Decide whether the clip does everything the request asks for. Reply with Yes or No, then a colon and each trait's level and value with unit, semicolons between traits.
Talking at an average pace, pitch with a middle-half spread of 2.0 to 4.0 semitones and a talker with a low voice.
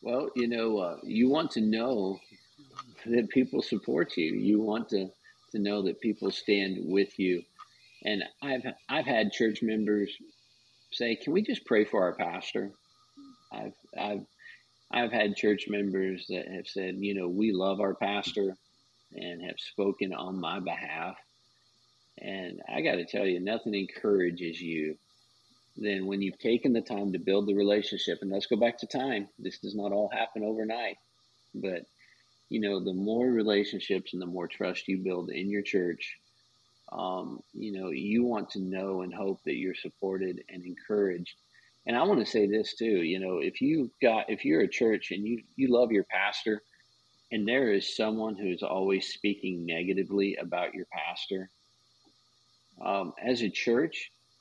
Yes: average, 170 wpm; average, 2.8 semitones; low, 100 Hz